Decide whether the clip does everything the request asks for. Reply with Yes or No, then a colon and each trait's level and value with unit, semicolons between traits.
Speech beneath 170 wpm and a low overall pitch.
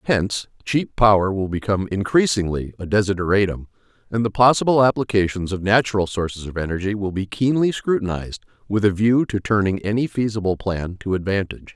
Yes: average, 160 wpm; low, 105 Hz